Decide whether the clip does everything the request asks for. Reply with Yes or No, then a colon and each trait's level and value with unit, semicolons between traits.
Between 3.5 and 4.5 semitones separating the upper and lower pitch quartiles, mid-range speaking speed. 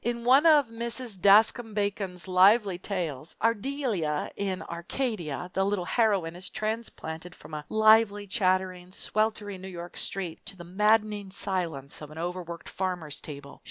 Yes: average, 3.8 semitones; average, 145 wpm